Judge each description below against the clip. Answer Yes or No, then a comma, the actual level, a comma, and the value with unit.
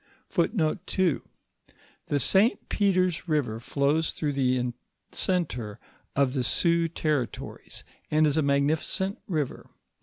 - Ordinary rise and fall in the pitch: Yes, average, 4.0 semitones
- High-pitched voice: No, medium, 150 Hz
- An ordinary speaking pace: No, slow, 110 wpm